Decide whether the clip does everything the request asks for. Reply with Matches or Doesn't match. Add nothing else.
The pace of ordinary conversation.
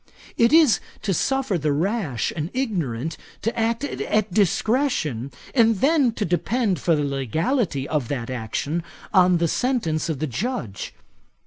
Matches